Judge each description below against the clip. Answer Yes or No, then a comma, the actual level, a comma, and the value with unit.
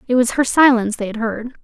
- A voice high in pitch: Yes, high, 235 Hz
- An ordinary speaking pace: No, fast, 255 wpm